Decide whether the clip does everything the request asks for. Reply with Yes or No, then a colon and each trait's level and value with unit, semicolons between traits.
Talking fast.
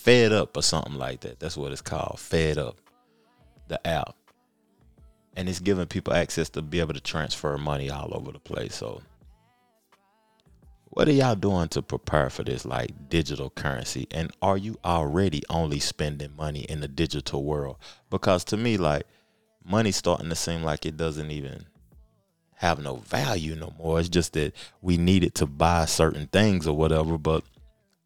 No: average, 175 wpm